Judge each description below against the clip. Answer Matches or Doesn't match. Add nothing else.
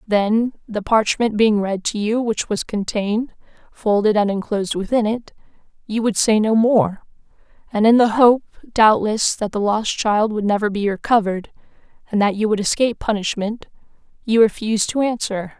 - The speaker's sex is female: Matches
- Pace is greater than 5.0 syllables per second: Doesn't match